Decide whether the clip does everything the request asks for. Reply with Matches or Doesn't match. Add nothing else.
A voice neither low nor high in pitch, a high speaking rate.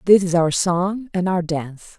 Matches